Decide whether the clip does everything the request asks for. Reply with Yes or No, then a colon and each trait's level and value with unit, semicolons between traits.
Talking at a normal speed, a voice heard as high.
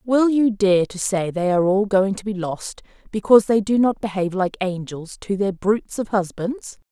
No: fast, 210 wpm; high, 200 Hz